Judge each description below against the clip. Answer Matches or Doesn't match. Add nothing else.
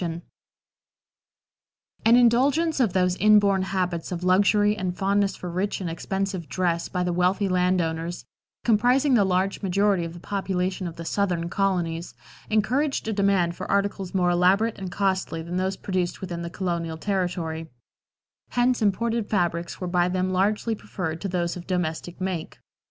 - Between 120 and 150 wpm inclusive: Doesn't match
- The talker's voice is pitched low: Doesn't match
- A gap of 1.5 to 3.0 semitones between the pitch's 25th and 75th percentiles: Matches